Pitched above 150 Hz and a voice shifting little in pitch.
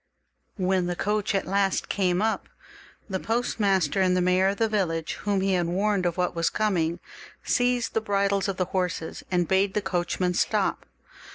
Yes: high, 190 Hz; narrow, 2.1 semitones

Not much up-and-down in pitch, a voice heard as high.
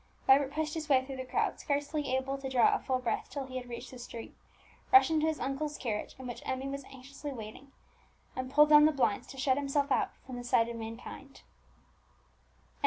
Yes: narrow, 2.2 semitones; very high, 270 Hz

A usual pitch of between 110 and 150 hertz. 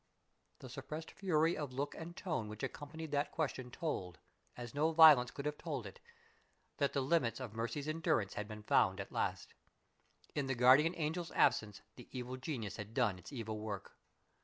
Yes: low, 135 Hz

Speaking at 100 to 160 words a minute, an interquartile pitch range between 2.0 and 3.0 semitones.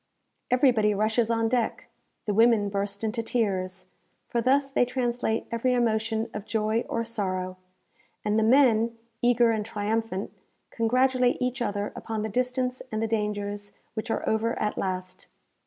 Yes: average, 150 wpm; narrow, 2.4 semitones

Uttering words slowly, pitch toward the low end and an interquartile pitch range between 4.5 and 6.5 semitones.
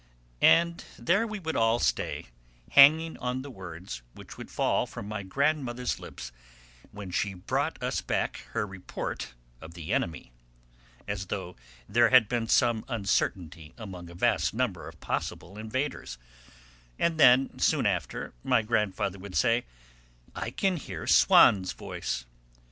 No: average, 145 wpm; low, 110 Hz; wide, 5.6 semitones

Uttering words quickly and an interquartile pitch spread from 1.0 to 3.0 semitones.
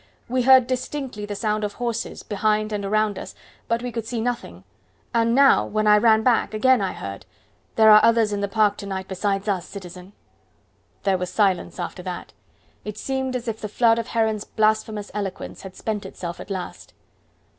No: average, 190 wpm; narrow, 2.6 semitones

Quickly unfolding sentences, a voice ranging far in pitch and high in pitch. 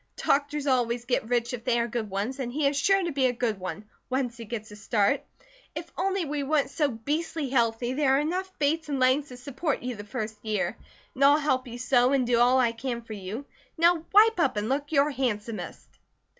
No: fast, 225 wpm; average, 3.6 semitones; very high, 255 Hz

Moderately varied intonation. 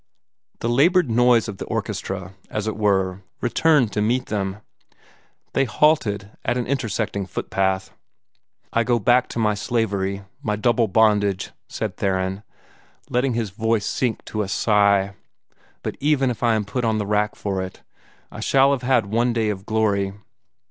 Yes: average, 3.4 semitones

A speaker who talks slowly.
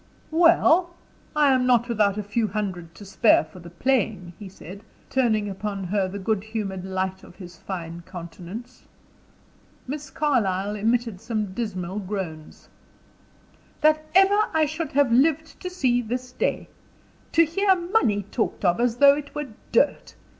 No: average, 155 wpm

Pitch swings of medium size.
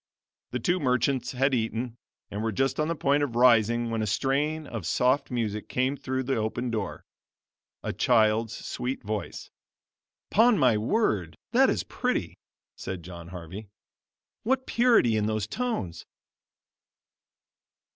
Yes: average, 4.2 semitones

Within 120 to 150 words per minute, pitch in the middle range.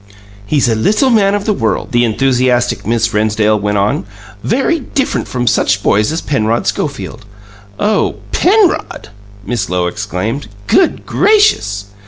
No: average, 140 wpm; low, 120 Hz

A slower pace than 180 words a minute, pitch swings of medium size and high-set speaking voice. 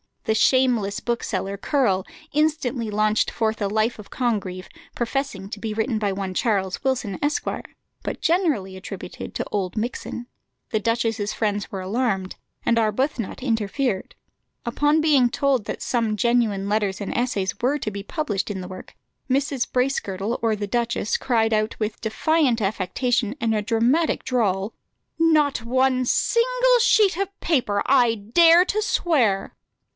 Yes: average, 145 wpm; average, 4.6 semitones; high, 230 Hz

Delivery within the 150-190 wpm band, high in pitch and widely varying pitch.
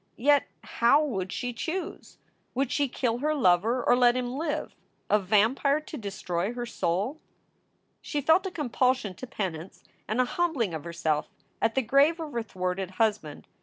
Yes: average, 165 wpm; high, 240 Hz; wide, 6.5 semitones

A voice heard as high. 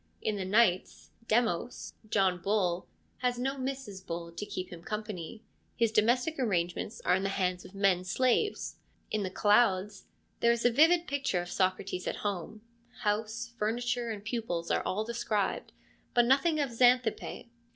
Yes: high, 215 Hz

